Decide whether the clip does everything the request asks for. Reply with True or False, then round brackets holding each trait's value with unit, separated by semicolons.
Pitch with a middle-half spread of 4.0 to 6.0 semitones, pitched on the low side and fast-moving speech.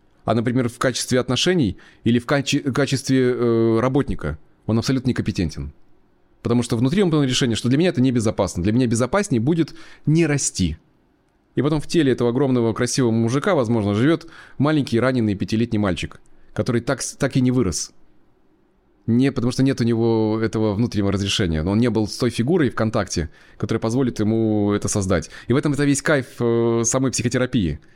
False (3.4 semitones; 120 Hz; 180 wpm)